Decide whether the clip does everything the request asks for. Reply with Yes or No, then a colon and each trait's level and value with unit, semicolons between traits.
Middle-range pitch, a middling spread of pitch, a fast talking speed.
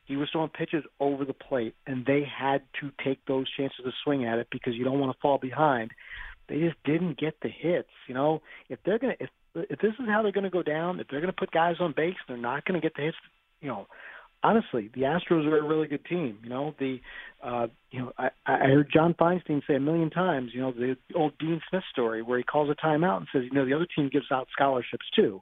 Yes: medium, 145 Hz; average, 3.7 semitones; fast, 250 wpm